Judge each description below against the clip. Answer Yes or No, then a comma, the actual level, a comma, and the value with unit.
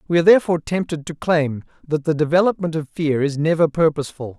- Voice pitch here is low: No, medium, 160 Hz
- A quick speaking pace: No, average, 190 wpm